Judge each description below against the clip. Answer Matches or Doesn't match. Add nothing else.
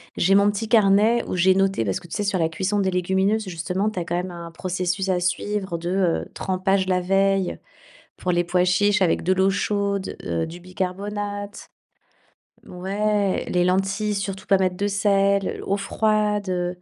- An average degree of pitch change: Doesn't match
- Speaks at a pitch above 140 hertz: Matches